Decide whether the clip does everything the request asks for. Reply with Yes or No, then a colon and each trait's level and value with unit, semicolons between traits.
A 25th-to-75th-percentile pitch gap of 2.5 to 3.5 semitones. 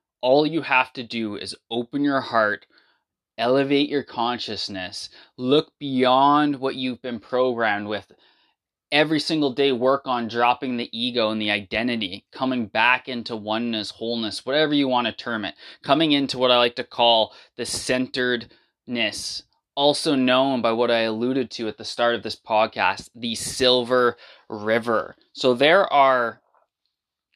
Yes: average, 2.9 semitones